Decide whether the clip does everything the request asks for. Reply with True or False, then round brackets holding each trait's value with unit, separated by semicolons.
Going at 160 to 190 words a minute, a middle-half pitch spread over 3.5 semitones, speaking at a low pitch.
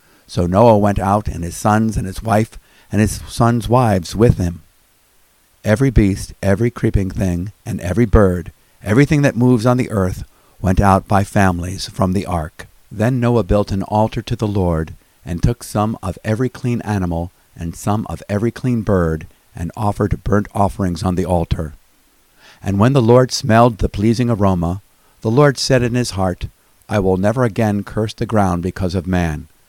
True (180 wpm; 4.0 semitones; 100 Hz)